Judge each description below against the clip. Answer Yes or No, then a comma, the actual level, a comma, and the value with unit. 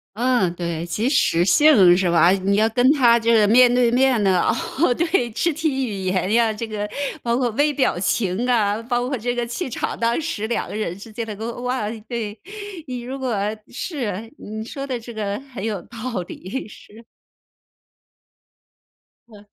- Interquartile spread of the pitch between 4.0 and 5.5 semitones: No, average, 3.5 semitones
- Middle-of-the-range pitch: No, high, 230 Hz